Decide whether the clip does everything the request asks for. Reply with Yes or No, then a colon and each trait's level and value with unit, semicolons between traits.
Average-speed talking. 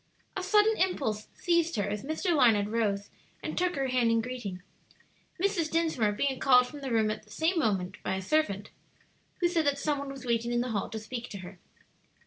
No: fast, 210 wpm